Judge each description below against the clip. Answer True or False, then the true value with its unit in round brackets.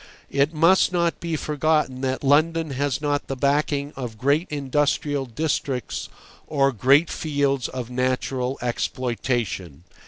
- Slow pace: True (125 wpm)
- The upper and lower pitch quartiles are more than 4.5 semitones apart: False (2.8 semitones)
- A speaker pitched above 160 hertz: False (140 Hz)